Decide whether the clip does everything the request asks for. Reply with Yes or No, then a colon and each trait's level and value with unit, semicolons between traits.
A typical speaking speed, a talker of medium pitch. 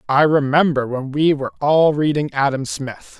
Yes: average, 170 wpm; medium, 145 Hz